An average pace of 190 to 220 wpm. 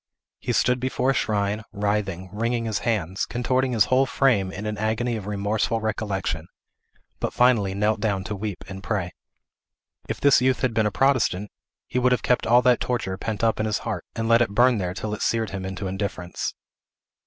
Yes: average, 200 wpm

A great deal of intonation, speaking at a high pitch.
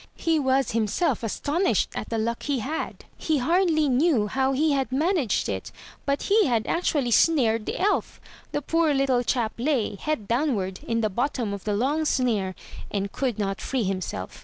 Yes: wide, 5.7 semitones; very high, 260 Hz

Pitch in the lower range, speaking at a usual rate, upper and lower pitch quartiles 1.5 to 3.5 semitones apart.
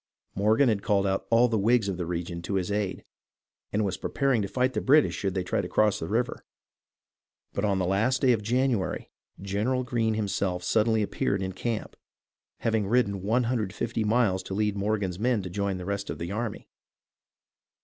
Yes: low, 105 Hz; average, 190 wpm; average, 3.2 semitones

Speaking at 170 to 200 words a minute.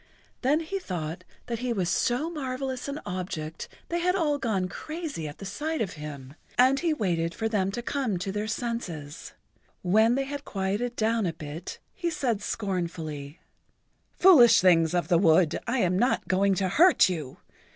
Yes: average, 175 wpm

